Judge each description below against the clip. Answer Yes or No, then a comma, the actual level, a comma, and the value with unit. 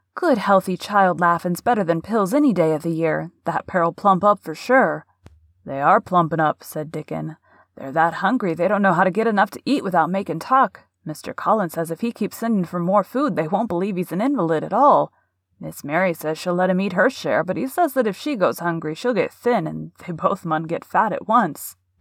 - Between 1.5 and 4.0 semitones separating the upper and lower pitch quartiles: No, average, 4.7 semitones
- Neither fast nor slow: No, fast, 230 wpm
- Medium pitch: Yes, medium, 180 Hz